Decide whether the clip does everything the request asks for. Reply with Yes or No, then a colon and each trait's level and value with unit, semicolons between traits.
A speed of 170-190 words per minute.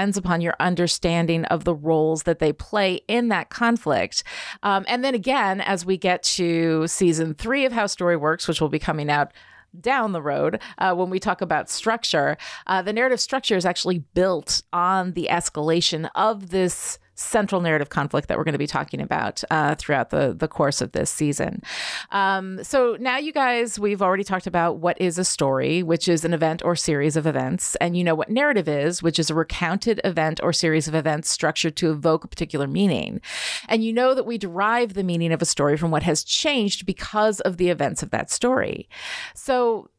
No: fast, 205 wpm